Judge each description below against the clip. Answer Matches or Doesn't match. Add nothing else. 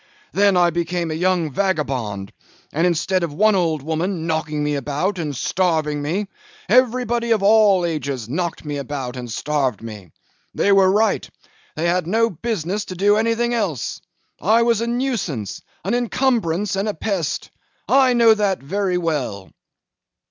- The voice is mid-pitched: Matches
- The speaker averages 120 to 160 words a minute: Matches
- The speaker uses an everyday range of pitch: Doesn't match